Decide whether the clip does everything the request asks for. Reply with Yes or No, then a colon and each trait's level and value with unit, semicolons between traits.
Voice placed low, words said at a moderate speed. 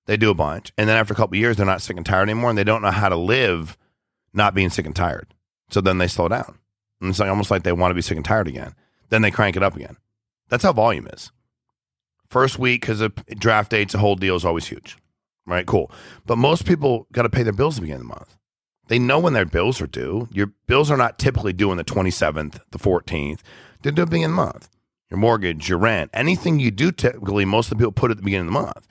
No: low, 105 Hz; fast, 270 wpm